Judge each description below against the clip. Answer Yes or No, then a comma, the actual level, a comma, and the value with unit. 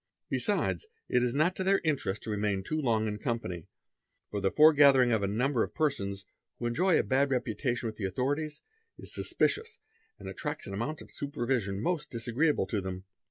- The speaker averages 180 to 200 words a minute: Yes, average, 185 wpm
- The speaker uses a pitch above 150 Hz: No, low, 125 Hz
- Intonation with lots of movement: Yes, wide, 6.0 semitones